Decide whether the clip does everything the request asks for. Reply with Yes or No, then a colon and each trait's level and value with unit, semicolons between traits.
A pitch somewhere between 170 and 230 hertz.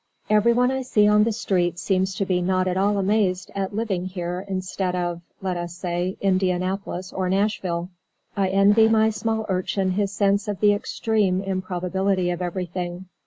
Yes: high, 190 Hz